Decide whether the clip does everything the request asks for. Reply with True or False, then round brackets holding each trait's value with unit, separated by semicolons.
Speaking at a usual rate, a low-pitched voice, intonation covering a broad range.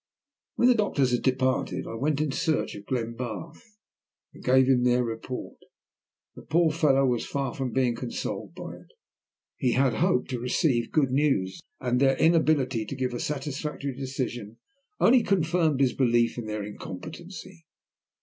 False (160 wpm; 130 Hz; 3.6 semitones)